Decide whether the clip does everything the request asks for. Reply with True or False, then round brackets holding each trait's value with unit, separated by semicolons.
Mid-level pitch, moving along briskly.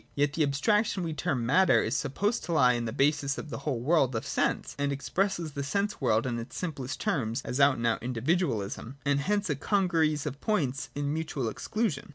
True (145 Hz; 210 wpm)